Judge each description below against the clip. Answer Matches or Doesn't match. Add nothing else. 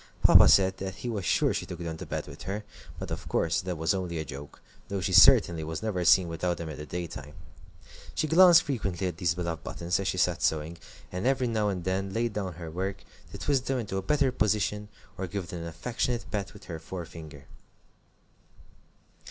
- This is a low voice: Matches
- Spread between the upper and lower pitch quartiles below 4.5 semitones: Matches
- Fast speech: Matches